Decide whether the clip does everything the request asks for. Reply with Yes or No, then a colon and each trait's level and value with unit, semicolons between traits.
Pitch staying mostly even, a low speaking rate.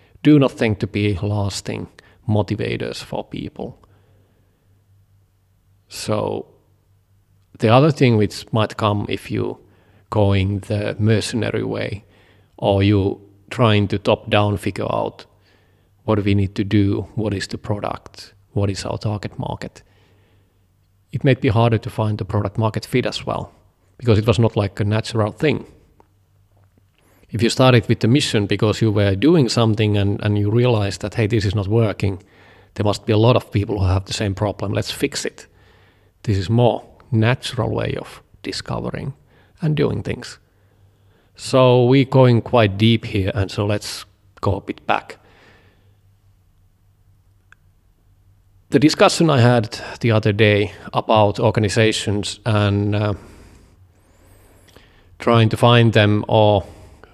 No: narrow, 2.3 semitones; average, 145 wpm